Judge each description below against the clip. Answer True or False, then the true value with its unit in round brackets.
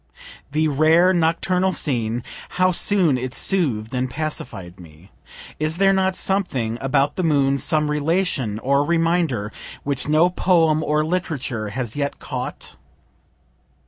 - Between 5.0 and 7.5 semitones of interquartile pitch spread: True (5.3 semitones)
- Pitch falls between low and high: True (150 Hz)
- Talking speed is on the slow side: True (130 wpm)